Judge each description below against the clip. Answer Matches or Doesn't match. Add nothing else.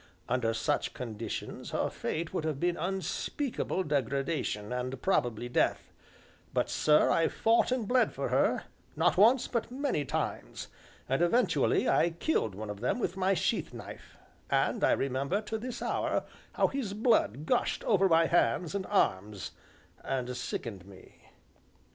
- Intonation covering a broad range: Matches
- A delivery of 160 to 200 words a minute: Doesn't match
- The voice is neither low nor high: Matches